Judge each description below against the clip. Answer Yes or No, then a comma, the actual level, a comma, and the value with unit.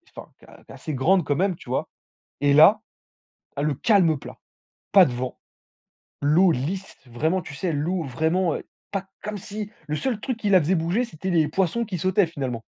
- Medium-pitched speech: Yes, medium, 170 Hz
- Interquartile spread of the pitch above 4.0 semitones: Yes, average, 4.8 semitones